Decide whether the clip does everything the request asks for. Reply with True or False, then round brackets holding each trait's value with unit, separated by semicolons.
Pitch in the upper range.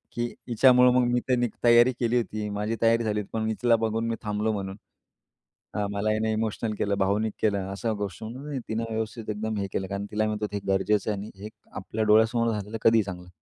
False (110 Hz)